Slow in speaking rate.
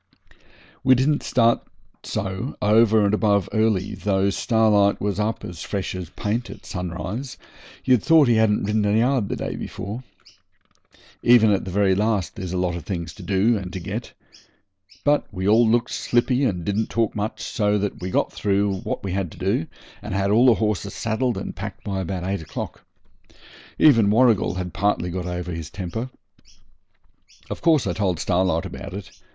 No: average, 180 wpm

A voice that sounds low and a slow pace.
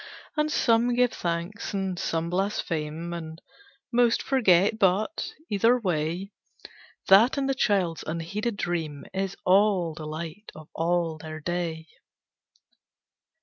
No: medium, 175 Hz; slow, 120 wpm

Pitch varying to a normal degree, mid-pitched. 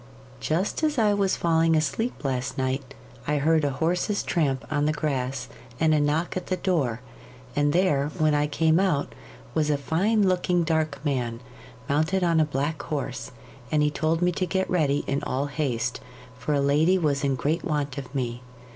Yes: average, 3.4 semitones; medium, 150 Hz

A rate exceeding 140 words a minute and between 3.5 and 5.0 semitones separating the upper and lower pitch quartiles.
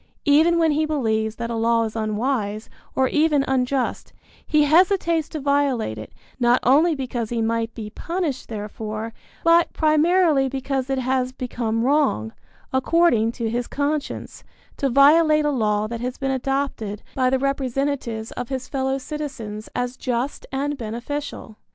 Yes: average, 150 wpm; average, 4.1 semitones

